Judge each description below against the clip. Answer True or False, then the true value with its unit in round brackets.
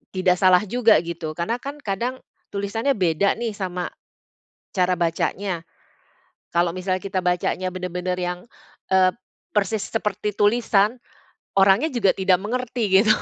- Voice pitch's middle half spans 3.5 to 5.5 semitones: False (3.1 semitones)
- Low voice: False (195 Hz)